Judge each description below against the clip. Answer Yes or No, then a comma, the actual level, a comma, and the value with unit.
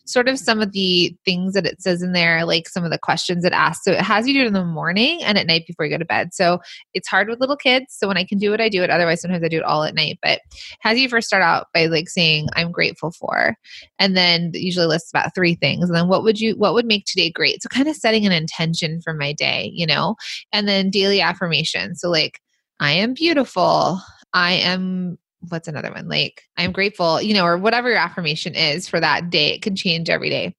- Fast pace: Yes, fast, 255 wpm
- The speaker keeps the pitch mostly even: No, average, 3.6 semitones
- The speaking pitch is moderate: Yes, medium, 180 Hz